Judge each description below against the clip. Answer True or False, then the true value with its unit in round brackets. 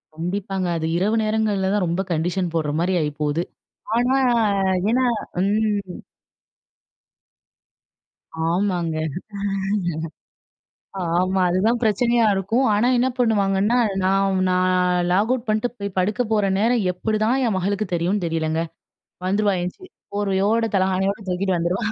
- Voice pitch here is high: True (195 Hz)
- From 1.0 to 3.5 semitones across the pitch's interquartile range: True (3.1 semitones)